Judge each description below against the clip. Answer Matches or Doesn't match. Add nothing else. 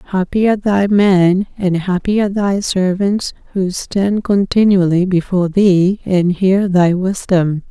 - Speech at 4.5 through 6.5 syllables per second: Doesn't match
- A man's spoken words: Doesn't match